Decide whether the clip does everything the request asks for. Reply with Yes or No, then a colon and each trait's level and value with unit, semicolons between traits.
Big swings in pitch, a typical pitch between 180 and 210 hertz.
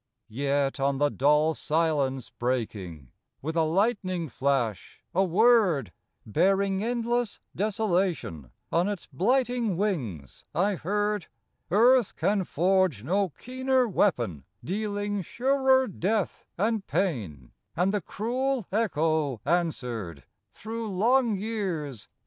Yes: wide, 7.3 semitones; medium, 185 Hz